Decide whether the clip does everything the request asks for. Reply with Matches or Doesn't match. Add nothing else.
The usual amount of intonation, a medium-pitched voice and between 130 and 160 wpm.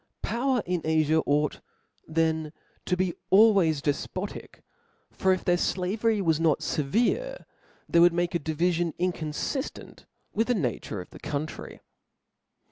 Matches